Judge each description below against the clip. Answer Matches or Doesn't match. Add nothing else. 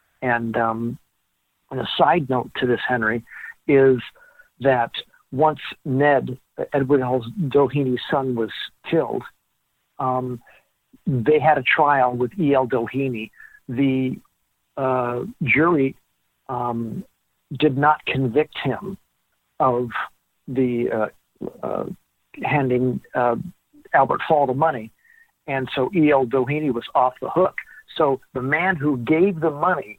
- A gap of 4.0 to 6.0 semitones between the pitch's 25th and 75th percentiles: Doesn't match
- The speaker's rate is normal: Doesn't match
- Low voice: Matches